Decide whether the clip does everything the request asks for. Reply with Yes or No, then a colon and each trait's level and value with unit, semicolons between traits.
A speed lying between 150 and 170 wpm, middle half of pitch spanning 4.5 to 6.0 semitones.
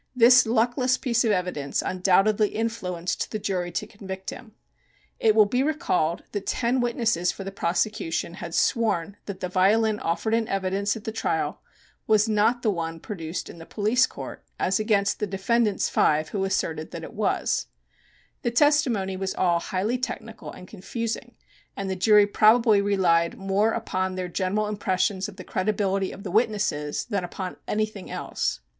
No: average, 165 wpm; average, 3.2 semitones